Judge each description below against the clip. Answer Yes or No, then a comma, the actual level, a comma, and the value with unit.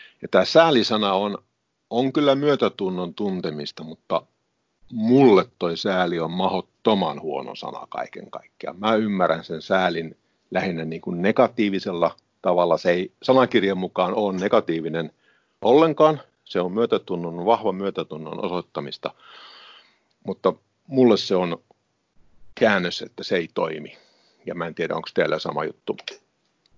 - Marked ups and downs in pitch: Yes, wide, 6.0 semitones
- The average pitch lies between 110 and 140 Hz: No, very low, 95 Hz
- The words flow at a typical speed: Yes, average, 125 wpm